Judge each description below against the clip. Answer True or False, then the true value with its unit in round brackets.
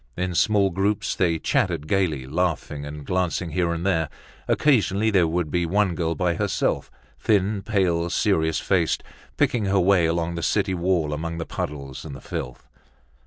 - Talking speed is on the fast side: False (165 wpm)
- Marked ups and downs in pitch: False (3.1 semitones)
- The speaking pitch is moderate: False (85 Hz)